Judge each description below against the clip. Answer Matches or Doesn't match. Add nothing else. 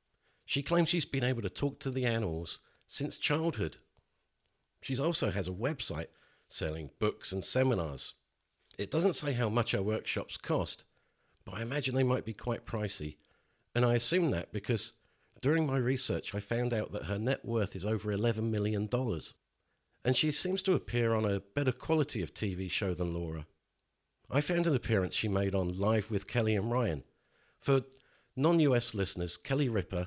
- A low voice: Matches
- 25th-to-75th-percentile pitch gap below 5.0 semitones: Doesn't match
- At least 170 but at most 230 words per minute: Matches